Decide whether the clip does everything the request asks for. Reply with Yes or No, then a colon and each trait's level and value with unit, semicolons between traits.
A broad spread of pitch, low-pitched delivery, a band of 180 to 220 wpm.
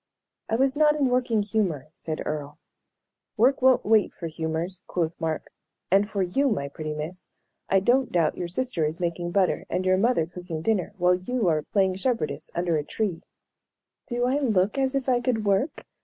No: wide, 6.5 semitones; high, 190 Hz; average, 185 wpm